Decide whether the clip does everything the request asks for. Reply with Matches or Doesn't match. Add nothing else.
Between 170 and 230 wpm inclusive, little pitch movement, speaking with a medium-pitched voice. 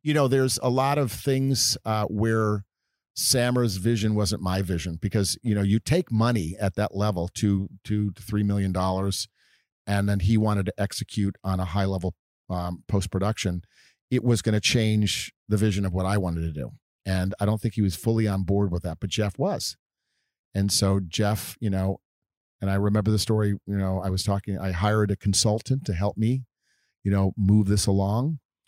Doesn't match